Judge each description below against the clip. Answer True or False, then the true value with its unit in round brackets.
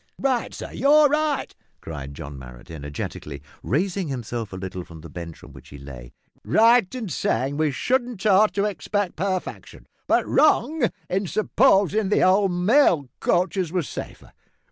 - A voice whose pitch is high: False (180 Hz)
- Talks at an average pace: True (155 wpm)